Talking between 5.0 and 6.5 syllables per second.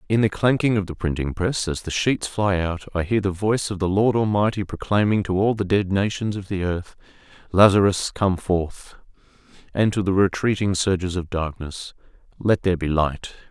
Yes: 5.1 syllables/s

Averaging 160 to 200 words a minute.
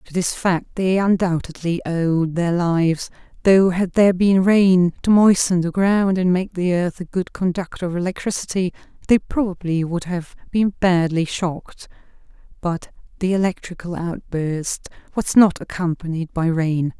No: average, 150 wpm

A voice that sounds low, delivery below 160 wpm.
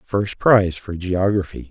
Yes: very low, 95 Hz; average, 140 wpm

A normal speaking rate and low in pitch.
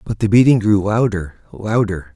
Yes: average, 165 wpm; low, 105 Hz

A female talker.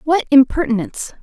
Yes: female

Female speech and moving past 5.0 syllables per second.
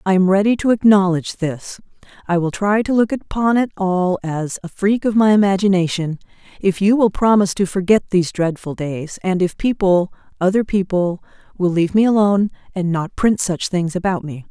Yes: female; 5.4 syllables/s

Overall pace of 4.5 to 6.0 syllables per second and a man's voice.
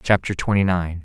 Yes: 5.4 syllables/s; male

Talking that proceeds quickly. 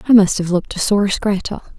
Yes: fast, 235 wpm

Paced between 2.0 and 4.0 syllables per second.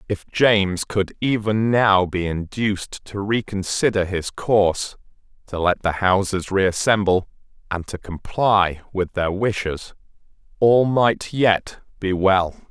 Yes: 3.8 syllables/s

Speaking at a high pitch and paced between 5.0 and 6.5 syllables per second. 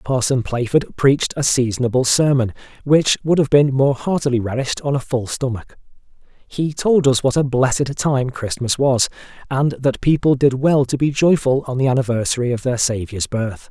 No: low, 130 Hz; 5.1 syllables/s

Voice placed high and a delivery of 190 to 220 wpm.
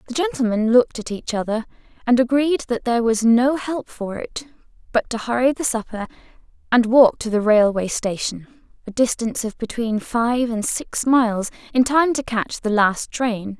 No: high, 235 Hz; average, 170 wpm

